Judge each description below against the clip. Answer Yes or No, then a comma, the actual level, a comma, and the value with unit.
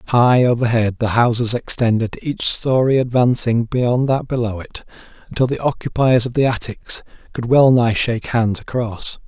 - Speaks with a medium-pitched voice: No, low, 120 Hz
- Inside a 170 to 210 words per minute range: No, average, 155 wpm